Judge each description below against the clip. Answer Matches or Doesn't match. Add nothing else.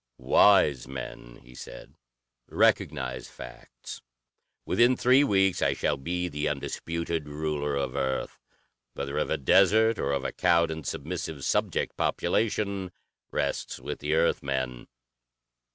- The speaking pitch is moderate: Doesn't match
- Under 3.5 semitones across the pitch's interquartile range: Doesn't match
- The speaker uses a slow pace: Matches